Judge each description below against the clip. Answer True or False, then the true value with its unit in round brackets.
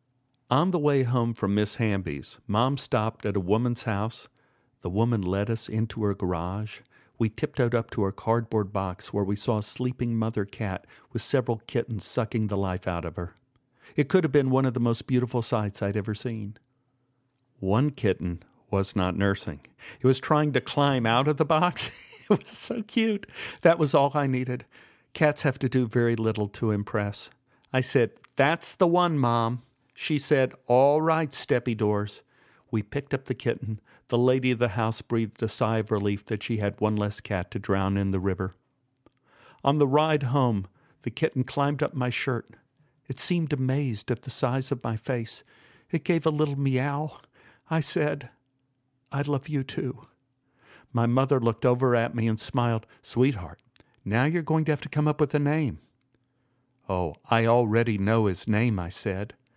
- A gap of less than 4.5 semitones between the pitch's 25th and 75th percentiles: True (4.1 semitones)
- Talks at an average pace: True (185 wpm)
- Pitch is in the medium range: False (125 Hz)